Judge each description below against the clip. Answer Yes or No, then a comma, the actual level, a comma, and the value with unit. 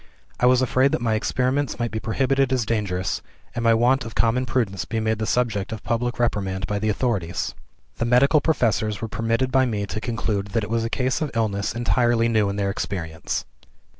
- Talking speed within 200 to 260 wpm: Yes, fast, 205 wpm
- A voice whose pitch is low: Yes, low, 115 Hz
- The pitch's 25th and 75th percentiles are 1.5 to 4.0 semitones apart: Yes, average, 3.1 semitones